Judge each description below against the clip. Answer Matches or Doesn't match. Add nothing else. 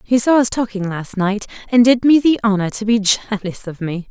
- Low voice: Doesn't match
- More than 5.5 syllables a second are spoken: Doesn't match